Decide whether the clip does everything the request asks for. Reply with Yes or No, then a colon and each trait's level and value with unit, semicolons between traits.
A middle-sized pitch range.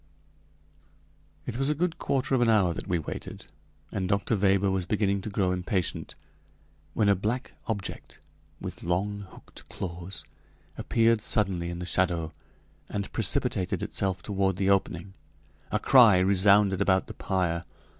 No: narrow, 2.3 semitones